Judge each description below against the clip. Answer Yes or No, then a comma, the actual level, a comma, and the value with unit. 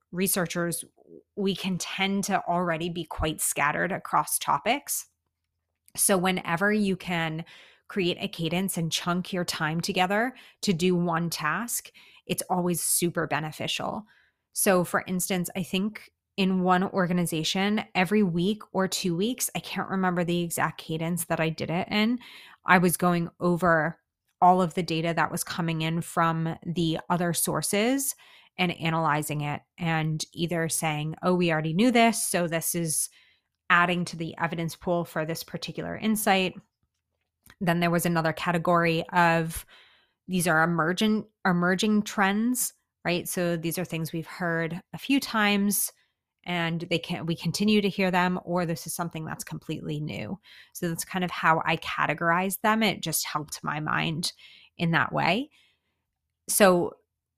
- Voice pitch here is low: No, medium, 175 Hz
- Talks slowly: No, average, 155 wpm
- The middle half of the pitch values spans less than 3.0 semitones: Yes, narrow, 2.5 semitones